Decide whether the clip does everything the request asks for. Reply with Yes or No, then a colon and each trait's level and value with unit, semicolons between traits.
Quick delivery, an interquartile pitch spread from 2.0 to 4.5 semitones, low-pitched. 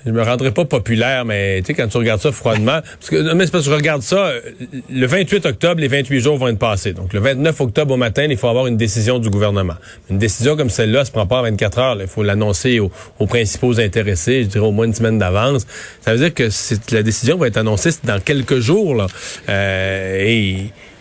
Yes: fast, 250 wpm; average, 4.1 semitones; low, 115 Hz